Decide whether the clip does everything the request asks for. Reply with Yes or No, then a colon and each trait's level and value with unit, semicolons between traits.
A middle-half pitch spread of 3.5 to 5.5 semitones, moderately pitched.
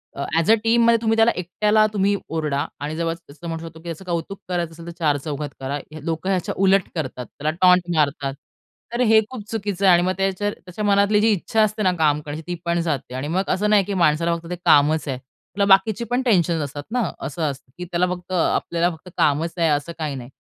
Yes: average, 4.6 semitones; medium, 170 Hz